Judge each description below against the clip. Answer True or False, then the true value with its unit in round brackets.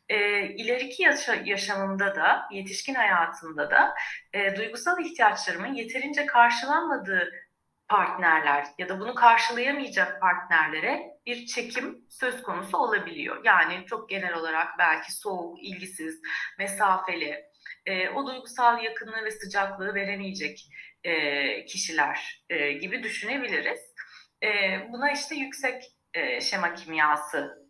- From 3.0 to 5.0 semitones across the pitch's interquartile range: False (5.5 semitones)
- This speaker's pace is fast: False (95 wpm)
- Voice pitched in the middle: False (210 Hz)